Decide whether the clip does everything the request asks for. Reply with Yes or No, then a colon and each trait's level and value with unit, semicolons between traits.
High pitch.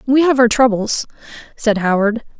Yes: high, 235 Hz